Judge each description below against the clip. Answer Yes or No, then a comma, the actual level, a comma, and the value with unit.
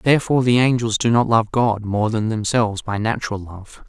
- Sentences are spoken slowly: No, average, 200 wpm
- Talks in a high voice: No, low, 115 Hz